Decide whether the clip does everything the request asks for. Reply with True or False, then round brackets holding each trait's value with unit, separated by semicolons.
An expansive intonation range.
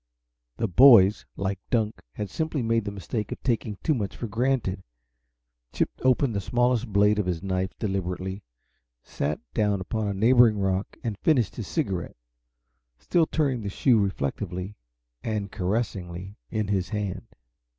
False (3.5 semitones)